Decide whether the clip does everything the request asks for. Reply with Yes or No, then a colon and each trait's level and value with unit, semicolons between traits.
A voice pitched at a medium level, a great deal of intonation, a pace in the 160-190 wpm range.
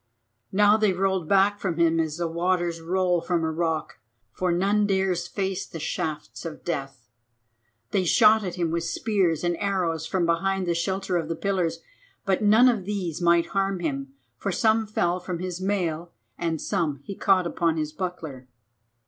No: medium, 175 Hz; average, 2.8 semitones; average, 175 wpm